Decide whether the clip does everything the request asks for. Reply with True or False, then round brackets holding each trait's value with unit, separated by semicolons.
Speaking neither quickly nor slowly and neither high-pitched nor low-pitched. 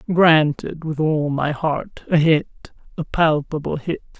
False (130 wpm; 155 Hz)